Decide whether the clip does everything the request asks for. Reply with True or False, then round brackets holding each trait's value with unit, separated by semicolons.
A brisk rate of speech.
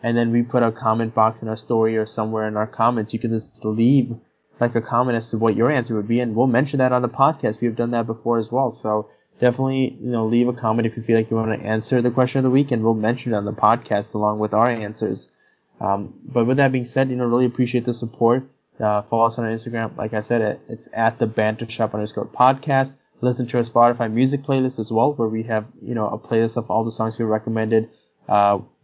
True (255 wpm)